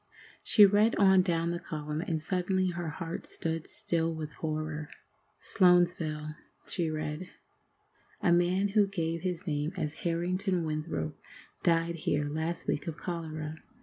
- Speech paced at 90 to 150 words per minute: Yes, average, 140 wpm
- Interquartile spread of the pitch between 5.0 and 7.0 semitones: No, average, 2.7 semitones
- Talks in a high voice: No, medium, 165 Hz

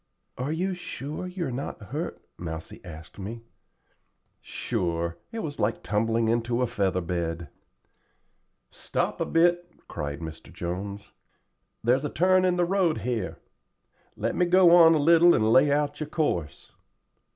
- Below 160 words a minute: Yes, average, 150 wpm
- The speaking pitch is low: Yes, low, 120 Hz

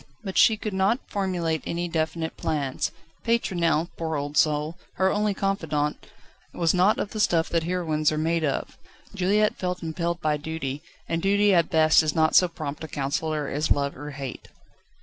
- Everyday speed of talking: Yes, average, 175 wpm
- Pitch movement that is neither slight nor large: Yes, average, 3.2 semitones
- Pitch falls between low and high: Yes, medium, 165 Hz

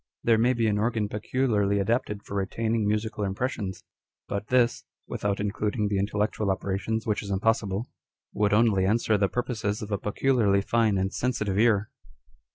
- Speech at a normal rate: Yes, average, 160 wpm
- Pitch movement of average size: No, narrow, 2.2 semitones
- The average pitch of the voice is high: No, low, 105 Hz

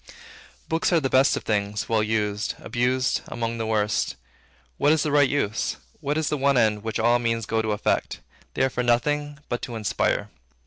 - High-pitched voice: No, low, 120 Hz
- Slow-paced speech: No, average, 195 wpm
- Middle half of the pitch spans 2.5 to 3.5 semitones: No, average, 4.2 semitones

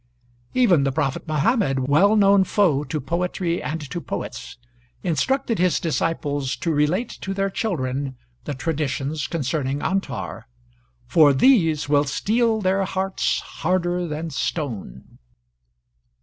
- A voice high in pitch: No, medium, 165 Hz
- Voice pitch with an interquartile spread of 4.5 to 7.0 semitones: Yes, average, 5.1 semitones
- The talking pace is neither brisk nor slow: No, slow, 120 wpm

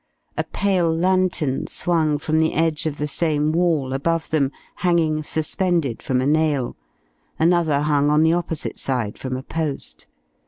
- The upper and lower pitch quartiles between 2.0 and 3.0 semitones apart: Yes, narrow, 2.5 semitones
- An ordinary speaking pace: Yes, average, 155 wpm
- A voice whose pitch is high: No, medium, 155 Hz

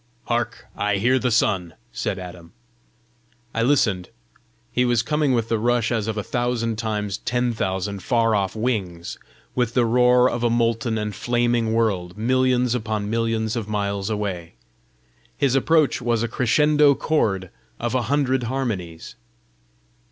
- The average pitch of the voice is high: No, low, 115 Hz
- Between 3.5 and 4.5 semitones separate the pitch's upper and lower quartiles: No, average, 3.0 semitones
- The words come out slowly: No, average, 150 wpm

